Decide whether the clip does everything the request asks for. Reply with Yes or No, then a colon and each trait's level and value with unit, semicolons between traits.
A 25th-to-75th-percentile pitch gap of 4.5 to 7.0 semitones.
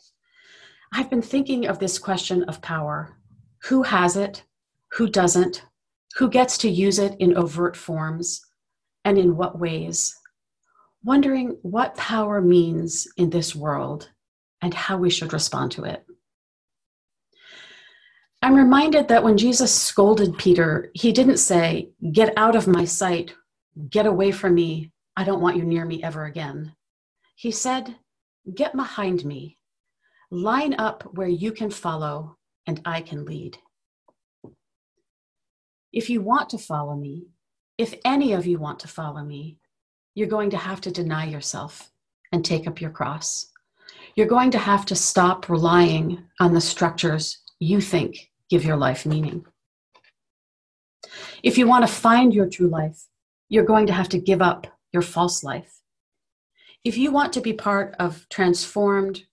Yes: average, 5.2 semitones